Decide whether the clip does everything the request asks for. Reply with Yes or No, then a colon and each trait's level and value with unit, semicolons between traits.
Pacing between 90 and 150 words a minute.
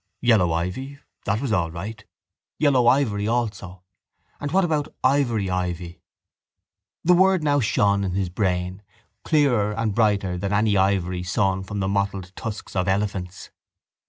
Yes: average, 145 wpm